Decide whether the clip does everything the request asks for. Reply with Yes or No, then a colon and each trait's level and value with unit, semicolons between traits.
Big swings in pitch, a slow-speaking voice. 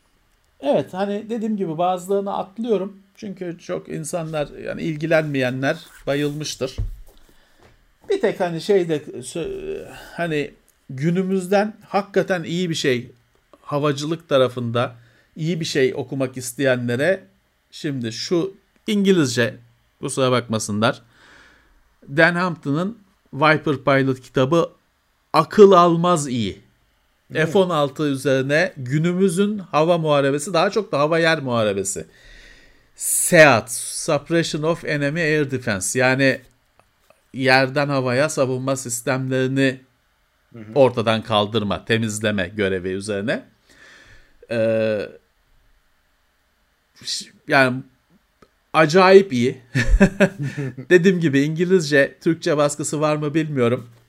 Yes: wide, 6.0 semitones; slow, 90 wpm